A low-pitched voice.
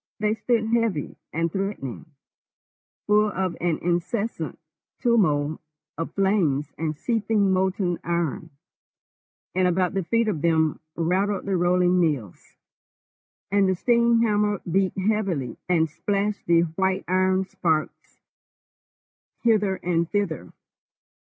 No: medium, 185 Hz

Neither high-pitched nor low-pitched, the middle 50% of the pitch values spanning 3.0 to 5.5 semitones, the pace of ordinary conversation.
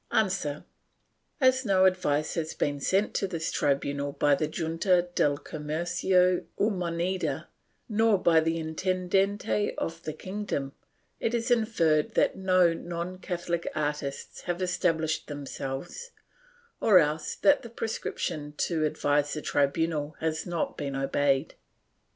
No: medium, 170 Hz; average, 3.9 semitones; slow, 130 wpm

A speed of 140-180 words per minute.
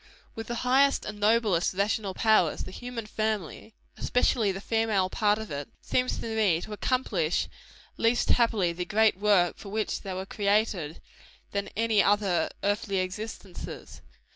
Yes: average, 150 wpm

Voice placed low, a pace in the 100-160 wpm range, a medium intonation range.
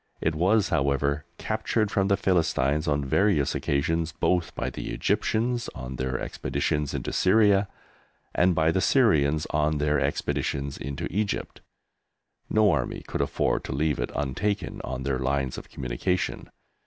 No: very low, 75 Hz; average, 145 wpm; wide, 5.8 semitones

